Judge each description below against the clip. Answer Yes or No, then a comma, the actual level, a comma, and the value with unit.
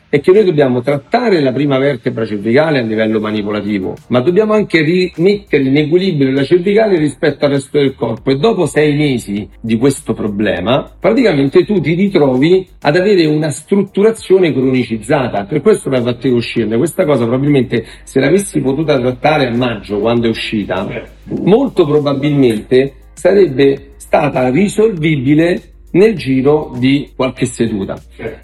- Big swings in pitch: Yes, wide, 5.9 semitones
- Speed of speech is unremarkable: Yes, average, 145 wpm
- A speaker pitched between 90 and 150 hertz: Yes, medium, 140 Hz